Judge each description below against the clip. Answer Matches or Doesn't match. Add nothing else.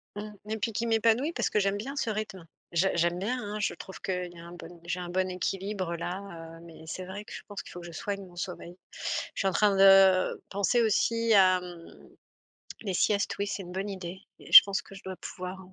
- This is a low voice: Doesn't match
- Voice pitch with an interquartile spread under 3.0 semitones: Matches